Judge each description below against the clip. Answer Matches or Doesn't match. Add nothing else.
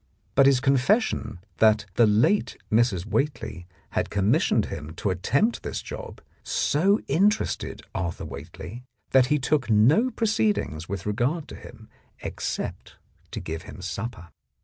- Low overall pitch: Matches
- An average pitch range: Doesn't match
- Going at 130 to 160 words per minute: Matches